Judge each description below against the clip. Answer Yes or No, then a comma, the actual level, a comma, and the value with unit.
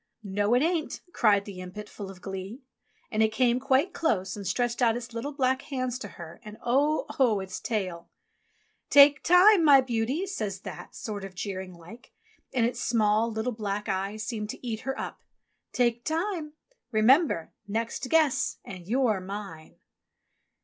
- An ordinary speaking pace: Yes, average, 165 wpm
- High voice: Yes, high, 225 Hz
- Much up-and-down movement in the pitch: No, average, 4.7 semitones